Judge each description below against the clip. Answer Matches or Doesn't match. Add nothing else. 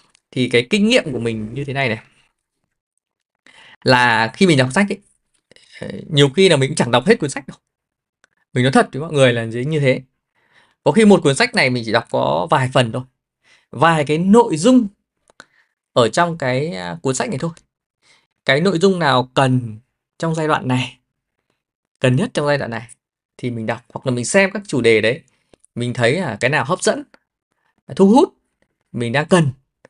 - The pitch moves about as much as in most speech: Doesn't match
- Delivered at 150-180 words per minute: Doesn't match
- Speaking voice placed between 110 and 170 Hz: Matches